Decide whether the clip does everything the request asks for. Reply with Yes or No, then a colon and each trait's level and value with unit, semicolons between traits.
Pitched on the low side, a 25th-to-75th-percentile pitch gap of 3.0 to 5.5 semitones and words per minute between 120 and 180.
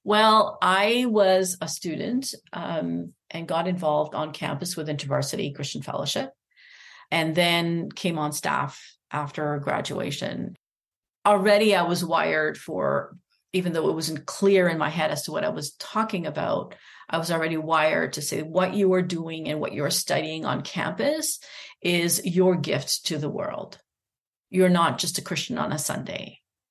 No: medium, 170 Hz; average, 3.8 semitones; average, 160 wpm